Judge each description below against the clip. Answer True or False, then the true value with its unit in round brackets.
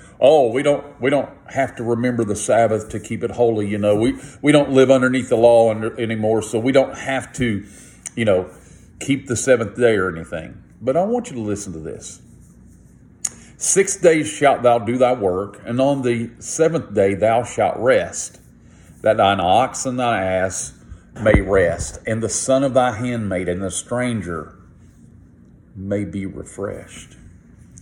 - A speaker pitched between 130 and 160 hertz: False (120 Hz)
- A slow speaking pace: False (175 wpm)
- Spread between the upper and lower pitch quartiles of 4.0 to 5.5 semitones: True (4.3 semitones)